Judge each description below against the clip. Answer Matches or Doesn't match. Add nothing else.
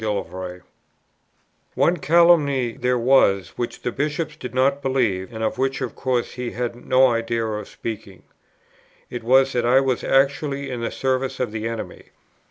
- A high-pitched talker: Doesn't match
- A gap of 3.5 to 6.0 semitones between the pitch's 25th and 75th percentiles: Doesn't match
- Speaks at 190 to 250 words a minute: Doesn't match